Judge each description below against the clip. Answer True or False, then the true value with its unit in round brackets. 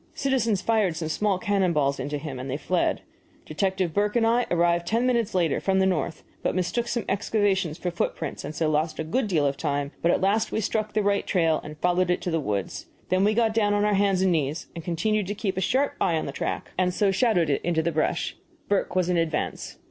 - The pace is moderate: False (240 wpm)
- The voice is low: False (185 Hz)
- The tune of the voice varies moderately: True (4.4 semitones)